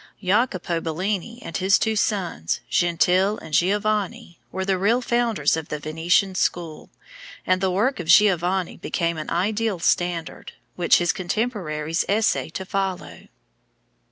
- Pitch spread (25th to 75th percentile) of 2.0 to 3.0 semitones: No, average, 3.6 semitones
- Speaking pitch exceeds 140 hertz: Yes, medium, 185 Hz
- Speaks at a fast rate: No, slow, 135 wpm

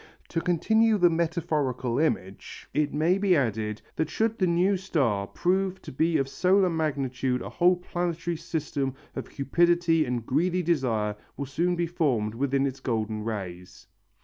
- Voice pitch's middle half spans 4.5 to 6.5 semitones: Yes, wide, 5.6 semitones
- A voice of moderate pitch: Yes, medium, 155 Hz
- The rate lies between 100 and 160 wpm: Yes, average, 155 wpm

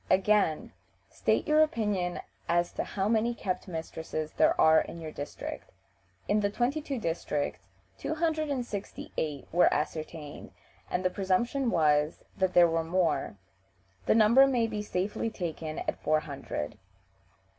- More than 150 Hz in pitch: Yes, medium, 185 Hz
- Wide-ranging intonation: Yes, wide, 6.1 semitones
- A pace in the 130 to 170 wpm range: Yes, average, 155 wpm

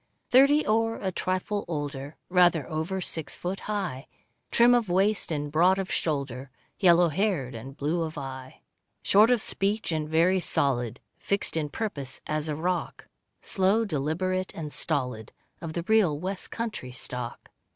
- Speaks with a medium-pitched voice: Yes, medium, 170 Hz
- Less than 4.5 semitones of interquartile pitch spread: No, average, 5.2 semitones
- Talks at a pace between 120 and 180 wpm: Yes, average, 150 wpm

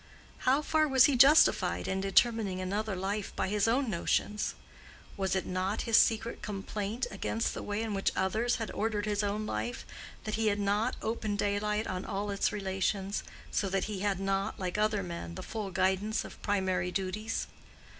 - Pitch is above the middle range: Yes, high, 205 Hz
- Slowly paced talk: No, average, 180 wpm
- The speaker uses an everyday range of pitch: No, narrow, 2.2 semitones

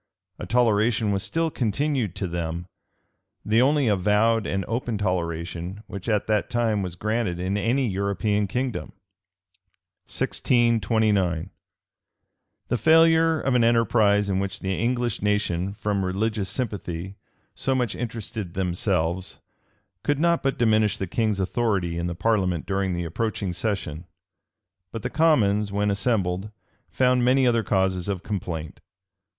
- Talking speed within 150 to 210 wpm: No, slow, 135 wpm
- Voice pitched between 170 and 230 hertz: No, low, 105 Hz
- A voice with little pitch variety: No, average, 3.8 semitones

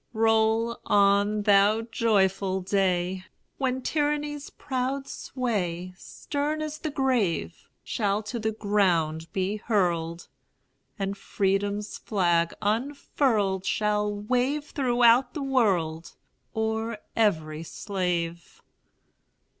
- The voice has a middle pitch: No, high, 210 Hz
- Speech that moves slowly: Yes, slow, 95 wpm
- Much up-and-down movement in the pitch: No, average, 4.5 semitones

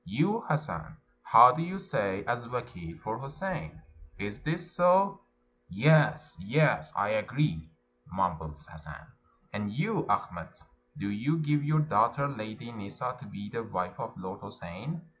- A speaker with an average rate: Yes, average, 160 wpm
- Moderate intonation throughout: No, wide, 8.2 semitones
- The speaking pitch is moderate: No, low, 120 Hz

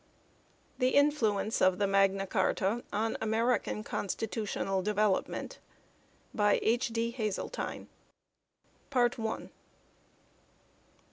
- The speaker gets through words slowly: Yes, slow, 80 wpm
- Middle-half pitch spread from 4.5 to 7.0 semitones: No, average, 3.0 semitones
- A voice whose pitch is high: Yes, high, 215 Hz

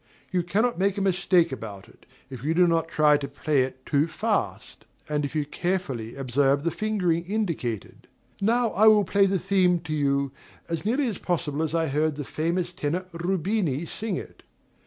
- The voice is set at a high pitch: No, medium, 165 Hz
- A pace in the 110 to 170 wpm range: No, average, 185 wpm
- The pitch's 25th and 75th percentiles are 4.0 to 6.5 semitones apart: Yes, average, 4.9 semitones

